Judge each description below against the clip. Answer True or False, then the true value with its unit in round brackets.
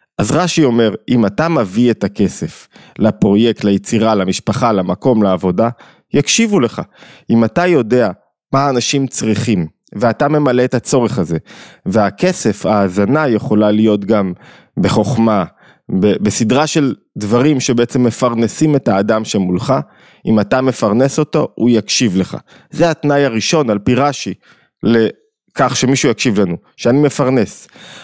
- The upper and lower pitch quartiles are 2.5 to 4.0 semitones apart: False (4.5 semitones)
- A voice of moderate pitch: False (115 Hz)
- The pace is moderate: True (130 wpm)